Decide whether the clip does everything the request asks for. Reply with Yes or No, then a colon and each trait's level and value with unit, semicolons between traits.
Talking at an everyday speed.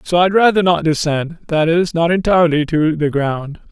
Yes: average, 180 wpm